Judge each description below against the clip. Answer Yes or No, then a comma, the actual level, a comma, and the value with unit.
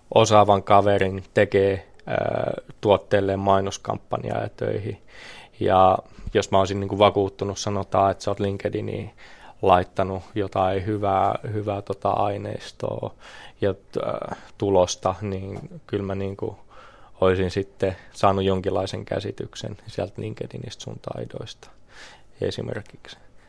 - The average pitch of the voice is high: No, low, 100 Hz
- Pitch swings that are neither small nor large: No, narrow, 1.0 semitones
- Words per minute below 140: Yes, average, 100 wpm